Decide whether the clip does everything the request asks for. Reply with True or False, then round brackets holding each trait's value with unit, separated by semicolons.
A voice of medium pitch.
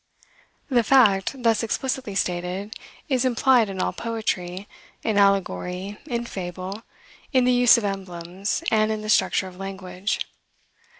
False (205 Hz)